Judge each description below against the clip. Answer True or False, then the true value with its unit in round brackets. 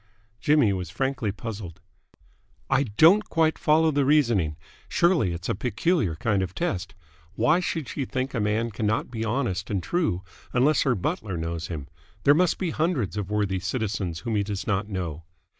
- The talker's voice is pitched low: True (110 Hz)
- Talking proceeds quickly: False (175 wpm)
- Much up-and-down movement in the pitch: True (7.0 semitones)